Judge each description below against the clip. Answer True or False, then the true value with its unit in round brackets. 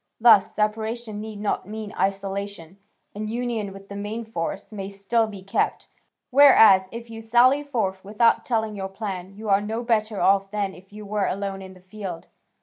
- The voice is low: False (210 Hz)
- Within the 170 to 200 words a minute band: True (180 wpm)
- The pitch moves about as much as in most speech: False (2.3 semitones)